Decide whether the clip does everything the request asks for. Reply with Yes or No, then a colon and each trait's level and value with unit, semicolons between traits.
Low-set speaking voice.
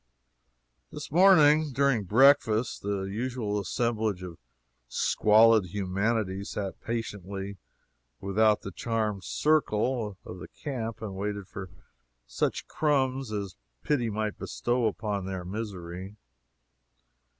Yes: low, 105 Hz